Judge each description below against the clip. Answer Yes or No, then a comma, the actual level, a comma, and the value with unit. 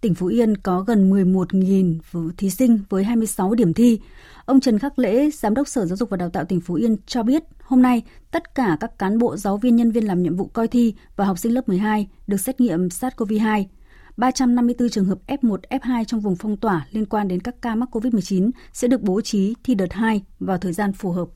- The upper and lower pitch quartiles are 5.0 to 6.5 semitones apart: No, average, 4.0 semitones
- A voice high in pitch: Yes, high, 220 Hz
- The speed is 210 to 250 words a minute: Yes, average, 230 wpm